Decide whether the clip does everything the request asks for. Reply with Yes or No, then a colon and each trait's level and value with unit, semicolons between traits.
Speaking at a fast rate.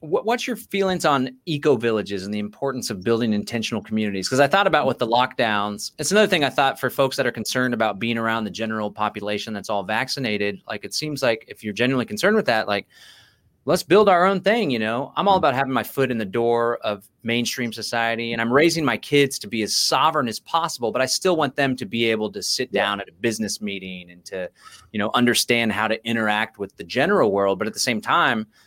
Yes: fast, 230 wpm